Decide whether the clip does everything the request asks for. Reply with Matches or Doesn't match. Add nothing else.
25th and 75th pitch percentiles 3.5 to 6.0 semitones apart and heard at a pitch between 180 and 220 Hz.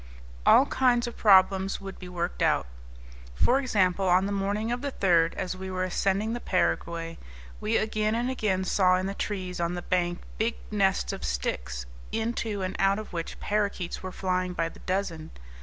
Doesn't match